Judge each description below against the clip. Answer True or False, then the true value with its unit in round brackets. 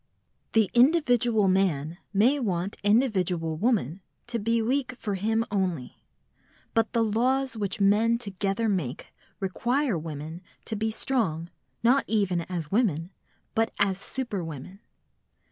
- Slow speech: True (125 wpm)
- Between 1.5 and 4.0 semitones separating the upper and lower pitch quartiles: False (4.4 semitones)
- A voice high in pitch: True (205 Hz)